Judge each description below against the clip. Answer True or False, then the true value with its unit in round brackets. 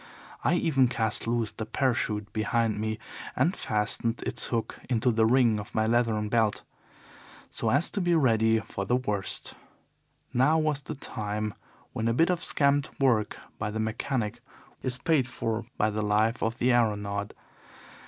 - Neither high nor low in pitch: False (115 Hz)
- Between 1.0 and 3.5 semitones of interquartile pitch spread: True (3.2 semitones)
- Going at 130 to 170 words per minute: True (165 wpm)